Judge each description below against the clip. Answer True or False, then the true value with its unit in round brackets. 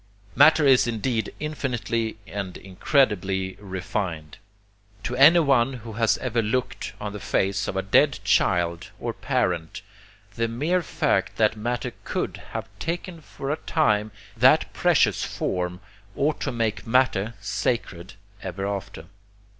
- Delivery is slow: True (130 wpm)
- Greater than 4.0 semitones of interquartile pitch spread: True (5.3 semitones)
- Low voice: True (110 Hz)